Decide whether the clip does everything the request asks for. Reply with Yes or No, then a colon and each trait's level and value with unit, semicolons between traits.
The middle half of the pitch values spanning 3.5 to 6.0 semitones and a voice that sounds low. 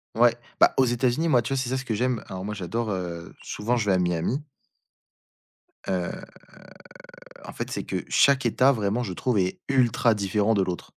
Yes: average, 5.0 semitones; low, 115 Hz